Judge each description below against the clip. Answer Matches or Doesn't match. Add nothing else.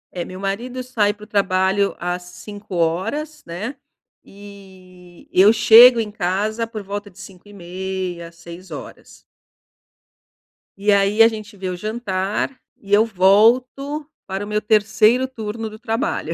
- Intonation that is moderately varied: Matches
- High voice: Matches